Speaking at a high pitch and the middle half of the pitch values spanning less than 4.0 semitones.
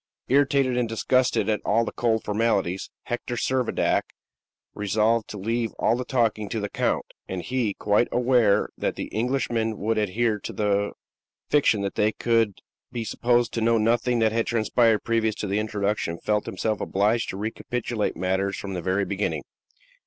No: low, 110 Hz; narrow, 2.6 semitones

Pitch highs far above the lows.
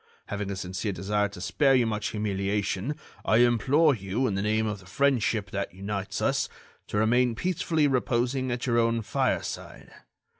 No: average, 4.0 semitones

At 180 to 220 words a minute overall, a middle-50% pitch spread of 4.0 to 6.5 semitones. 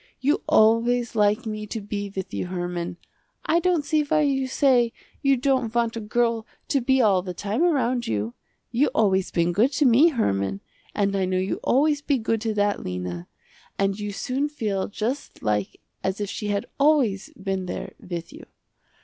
Yes: average, 185 wpm; wide, 5.5 semitones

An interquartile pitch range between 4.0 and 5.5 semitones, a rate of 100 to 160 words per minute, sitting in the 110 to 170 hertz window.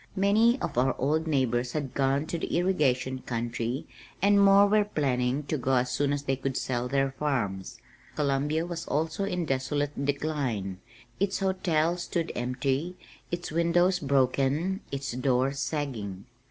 Yes: average, 4.7 semitones; average, 150 wpm; medium, 140 Hz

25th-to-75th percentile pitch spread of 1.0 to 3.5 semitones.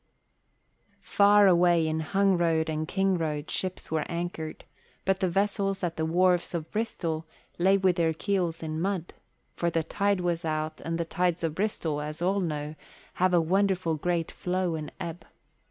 Yes: average, 2.8 semitones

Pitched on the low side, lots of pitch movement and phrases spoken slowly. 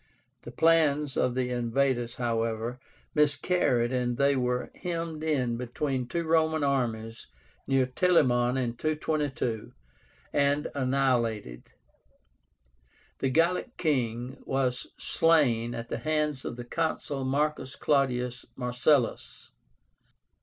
No: low, 130 Hz; average, 3.7 semitones; slow, 105 wpm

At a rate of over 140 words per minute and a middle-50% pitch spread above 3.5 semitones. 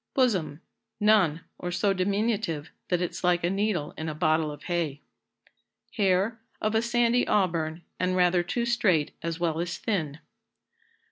Yes: average, 150 wpm; average, 4.4 semitones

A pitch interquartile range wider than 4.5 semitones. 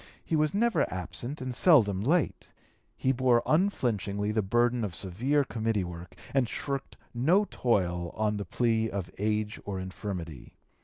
Yes: average, 5.1 semitones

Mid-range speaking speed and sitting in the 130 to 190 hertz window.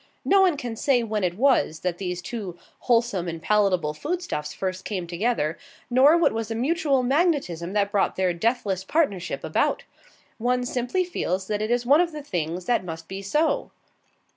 No: average, 185 wpm; high, 215 Hz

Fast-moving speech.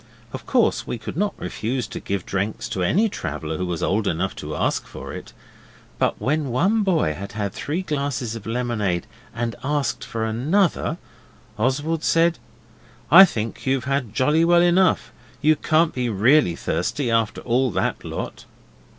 No: average, 165 wpm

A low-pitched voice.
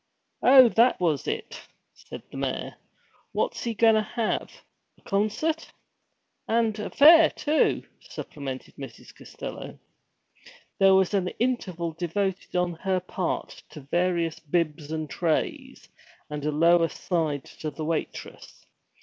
No: medium, 180 Hz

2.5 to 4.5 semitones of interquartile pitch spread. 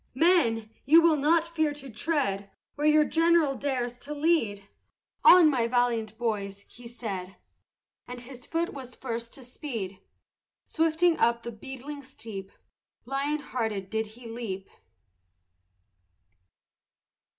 No: average, 5.1 semitones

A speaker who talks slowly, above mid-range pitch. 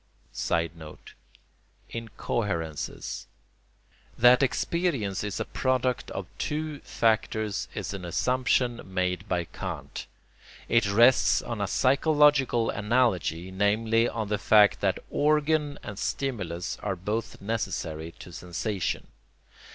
No: slow, 105 wpm; low, 110 Hz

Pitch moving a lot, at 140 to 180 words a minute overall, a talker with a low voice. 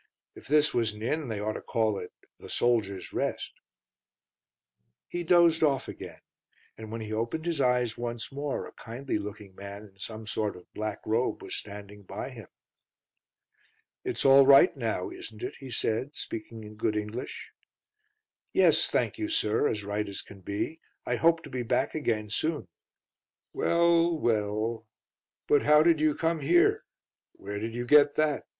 Yes: wide, 5.8 semitones; average, 170 wpm; low, 115 Hz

